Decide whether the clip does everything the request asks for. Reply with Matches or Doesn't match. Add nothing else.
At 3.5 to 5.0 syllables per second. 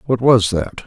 Matches